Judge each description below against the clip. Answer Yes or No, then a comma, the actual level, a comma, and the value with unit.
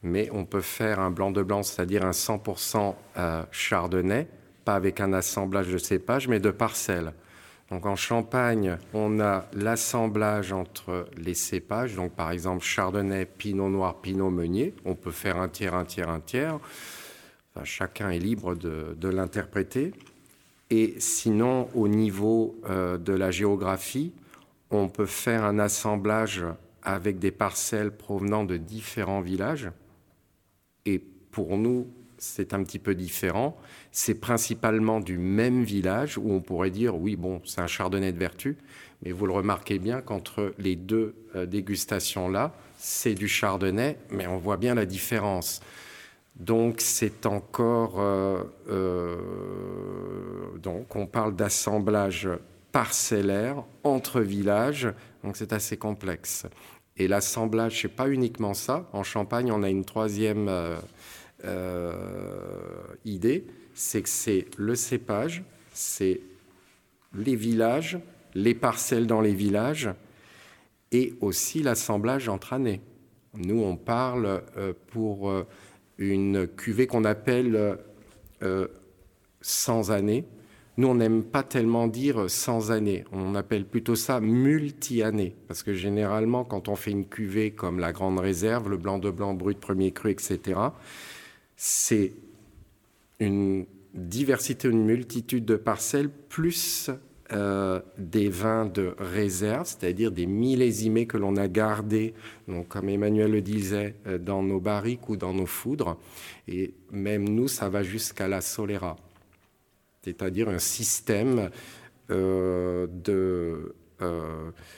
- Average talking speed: No, slow, 135 wpm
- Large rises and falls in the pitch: No, average, 3.2 semitones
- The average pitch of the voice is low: Yes, low, 100 Hz